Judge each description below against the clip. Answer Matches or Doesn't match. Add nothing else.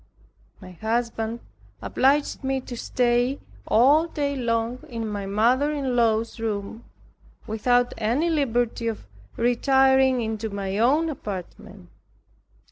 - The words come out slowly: Matches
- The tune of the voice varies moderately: Matches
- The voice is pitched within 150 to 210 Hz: Doesn't match